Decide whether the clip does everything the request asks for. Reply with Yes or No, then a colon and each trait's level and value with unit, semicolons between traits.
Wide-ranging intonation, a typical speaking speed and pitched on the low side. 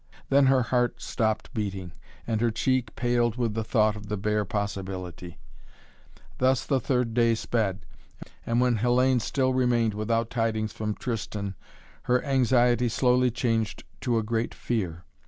No: average, 2.7 semitones; average, 150 wpm; low, 115 Hz